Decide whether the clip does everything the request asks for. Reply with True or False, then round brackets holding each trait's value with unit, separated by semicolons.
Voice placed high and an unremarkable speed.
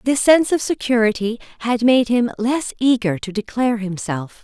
True (235 Hz; 160 wpm)